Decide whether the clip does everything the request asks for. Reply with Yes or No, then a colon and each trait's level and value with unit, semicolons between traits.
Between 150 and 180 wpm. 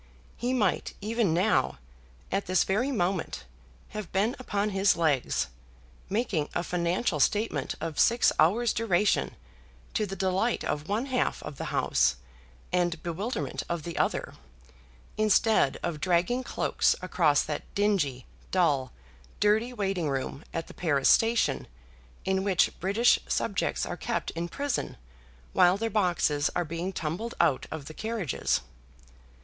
No: average, 140 wpm